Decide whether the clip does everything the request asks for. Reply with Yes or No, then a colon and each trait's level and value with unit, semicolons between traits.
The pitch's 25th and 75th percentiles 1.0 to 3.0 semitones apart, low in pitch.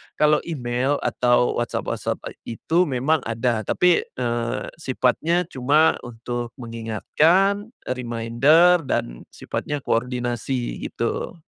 No: average, 4.7 semitones; low, 125 Hz